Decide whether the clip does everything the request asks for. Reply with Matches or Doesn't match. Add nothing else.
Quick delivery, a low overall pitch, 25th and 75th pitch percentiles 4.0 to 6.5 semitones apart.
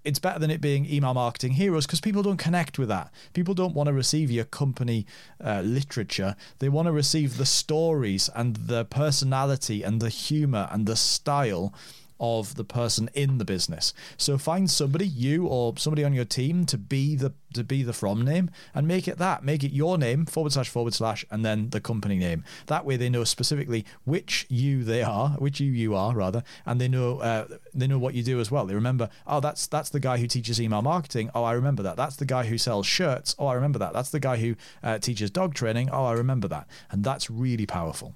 Matches